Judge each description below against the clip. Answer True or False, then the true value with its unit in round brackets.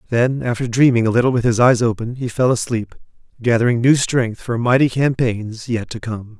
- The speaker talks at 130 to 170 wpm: False (195 wpm)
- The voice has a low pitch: True (120 Hz)